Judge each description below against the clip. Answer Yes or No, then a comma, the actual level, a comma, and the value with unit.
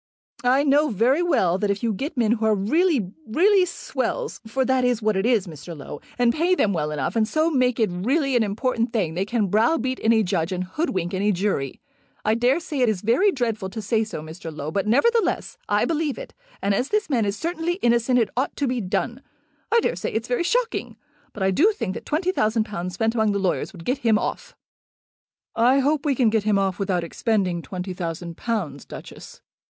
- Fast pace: Yes, fast, 215 wpm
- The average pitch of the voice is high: Yes, high, 225 Hz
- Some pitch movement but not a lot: No, wide, 5.8 semitones